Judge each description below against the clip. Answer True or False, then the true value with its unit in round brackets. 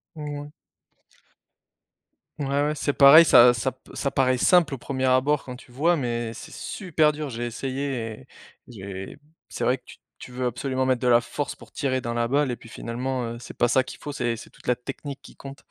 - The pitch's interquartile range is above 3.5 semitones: False (2.9 semitones)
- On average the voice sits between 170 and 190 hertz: False (130 Hz)